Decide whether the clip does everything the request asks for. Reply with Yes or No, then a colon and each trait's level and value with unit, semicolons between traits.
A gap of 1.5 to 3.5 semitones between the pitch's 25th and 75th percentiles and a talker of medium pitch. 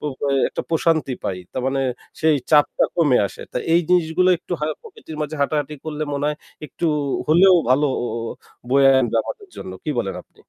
Yes: average, 3.0 semitones; medium, 150 Hz